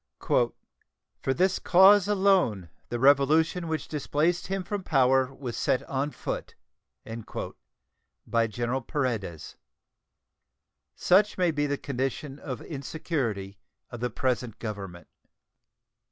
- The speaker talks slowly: Yes, slow, 110 wpm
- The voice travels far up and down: Yes, wide, 5.7 semitones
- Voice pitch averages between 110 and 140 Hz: Yes, low, 135 Hz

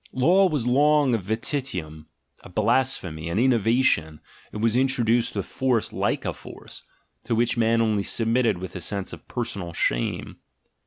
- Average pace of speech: Yes, average, 155 wpm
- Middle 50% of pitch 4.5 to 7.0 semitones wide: Yes, average, 5.2 semitones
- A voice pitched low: Yes, low, 115 Hz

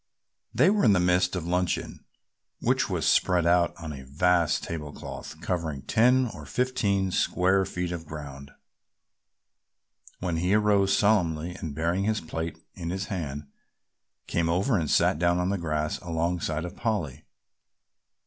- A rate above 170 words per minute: No, average, 150 wpm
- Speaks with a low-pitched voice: Yes, very low, 90 Hz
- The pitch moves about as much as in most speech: Yes, average, 3.3 semitones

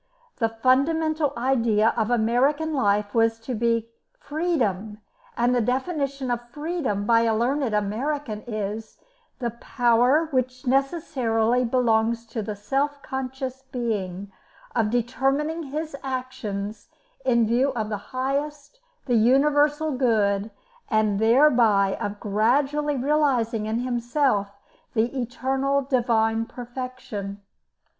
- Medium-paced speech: No, slow, 115 wpm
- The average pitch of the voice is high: Yes, high, 245 Hz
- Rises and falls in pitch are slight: No, average, 3.7 semitones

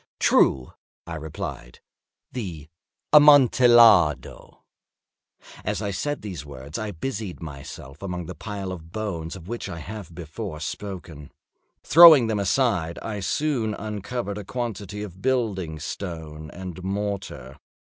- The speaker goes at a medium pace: No, slow, 125 wpm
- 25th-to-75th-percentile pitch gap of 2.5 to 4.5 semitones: No, average, 5.2 semitones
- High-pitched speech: No, very low, 95 Hz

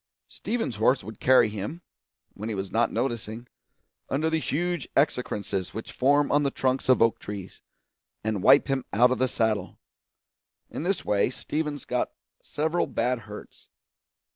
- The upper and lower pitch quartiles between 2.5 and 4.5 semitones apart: No, average, 4.9 semitones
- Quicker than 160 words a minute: No, average, 155 wpm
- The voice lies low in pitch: Yes, low, 125 Hz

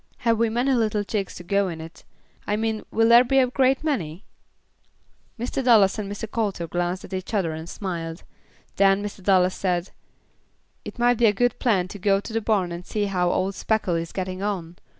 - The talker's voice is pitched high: Yes, high, 200 Hz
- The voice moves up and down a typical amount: Yes, average, 3.9 semitones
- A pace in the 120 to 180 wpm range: No, fast, 205 wpm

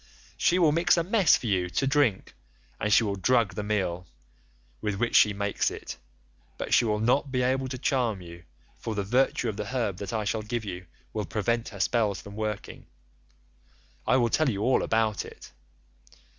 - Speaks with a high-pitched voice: No, low, 110 Hz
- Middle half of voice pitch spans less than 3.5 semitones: No, average, 3.9 semitones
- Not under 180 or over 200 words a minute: Yes, average, 195 wpm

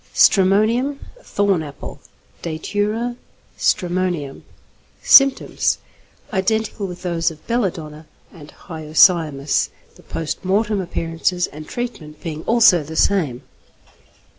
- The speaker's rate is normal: No, slow, 100 wpm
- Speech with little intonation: No, average, 4.8 semitones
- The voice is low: No, medium, 180 Hz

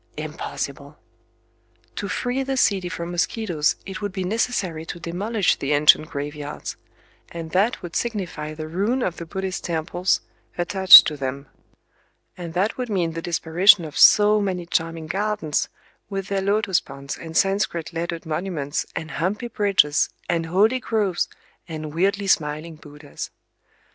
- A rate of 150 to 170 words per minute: No, average, 140 wpm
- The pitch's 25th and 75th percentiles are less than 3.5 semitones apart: No, average, 4.0 semitones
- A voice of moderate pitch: Yes, medium, 175 Hz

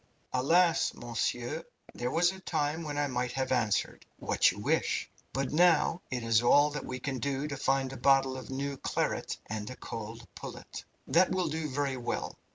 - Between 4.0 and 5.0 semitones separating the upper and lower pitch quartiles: No, average, 3.3 semitones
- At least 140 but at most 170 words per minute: No, average, 185 wpm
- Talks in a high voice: No, low, 135 Hz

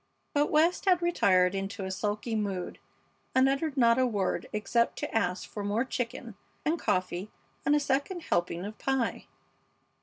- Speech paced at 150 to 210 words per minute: Yes, average, 160 wpm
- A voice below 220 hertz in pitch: No, high, 230 Hz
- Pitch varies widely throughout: Yes, wide, 5.8 semitones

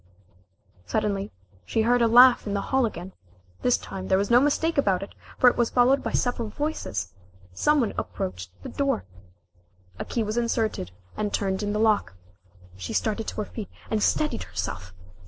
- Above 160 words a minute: Yes, average, 180 wpm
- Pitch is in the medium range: No, high, 215 Hz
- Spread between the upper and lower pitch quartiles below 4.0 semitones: No, average, 4.3 semitones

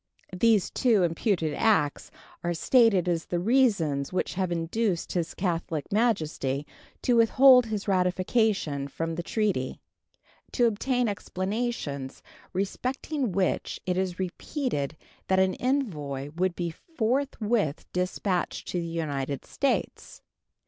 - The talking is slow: Yes, slow, 120 wpm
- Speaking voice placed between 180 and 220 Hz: Yes, medium, 185 Hz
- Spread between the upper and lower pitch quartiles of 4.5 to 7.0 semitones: Yes, wide, 5.6 semitones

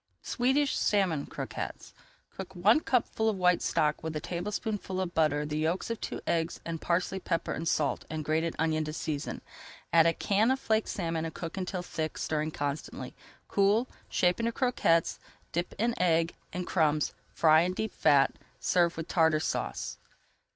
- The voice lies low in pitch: No, medium, 170 Hz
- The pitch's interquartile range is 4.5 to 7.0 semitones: No, average, 4.0 semitones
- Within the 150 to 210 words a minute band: Yes, average, 170 wpm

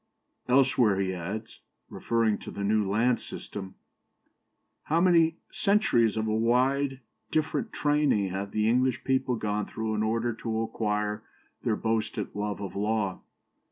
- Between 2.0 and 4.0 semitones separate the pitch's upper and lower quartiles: Yes, average, 3.6 semitones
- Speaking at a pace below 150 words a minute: Yes, average, 140 wpm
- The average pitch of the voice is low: Yes, low, 110 Hz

